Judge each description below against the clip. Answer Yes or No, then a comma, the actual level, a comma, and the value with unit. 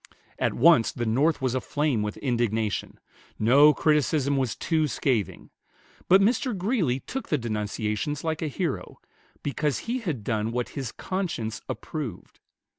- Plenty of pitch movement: Yes, wide, 5.7 semitones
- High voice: No, low, 135 Hz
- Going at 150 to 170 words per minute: No, average, 140 wpm